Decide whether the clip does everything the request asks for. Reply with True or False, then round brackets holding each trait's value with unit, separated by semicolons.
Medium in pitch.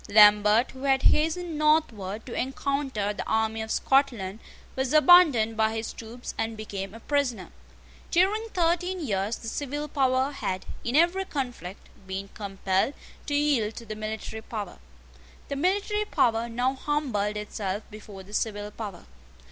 False (230 Hz)